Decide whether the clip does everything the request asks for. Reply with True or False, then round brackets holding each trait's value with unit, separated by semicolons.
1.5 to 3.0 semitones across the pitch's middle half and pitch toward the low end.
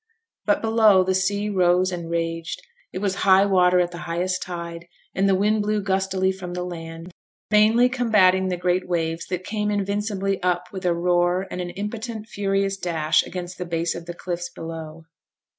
False (2.4 semitones; 185 Hz)